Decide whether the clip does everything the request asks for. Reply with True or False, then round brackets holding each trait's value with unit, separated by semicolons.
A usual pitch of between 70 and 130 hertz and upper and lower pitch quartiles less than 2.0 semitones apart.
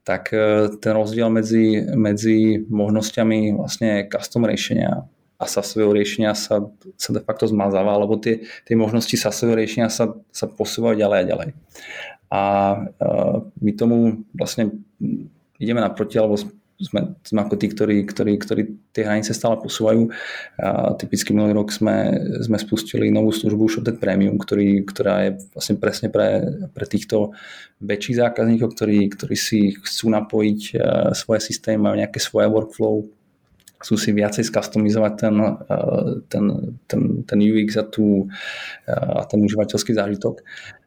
True (110 Hz; 1.2 semitones)